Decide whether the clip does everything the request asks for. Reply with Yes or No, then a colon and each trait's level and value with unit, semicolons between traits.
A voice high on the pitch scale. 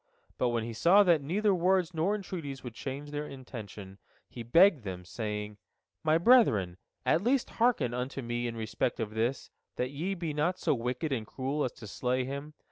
No: low, 135 Hz